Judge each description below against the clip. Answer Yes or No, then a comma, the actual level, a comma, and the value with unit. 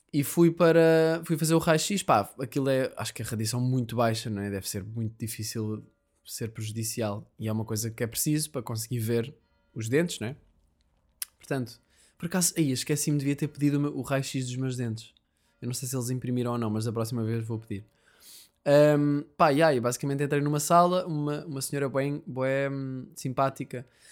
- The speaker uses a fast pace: Yes, fast, 200 wpm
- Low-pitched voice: Yes, low, 130 Hz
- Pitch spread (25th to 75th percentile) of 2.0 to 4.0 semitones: No, average, 4.4 semitones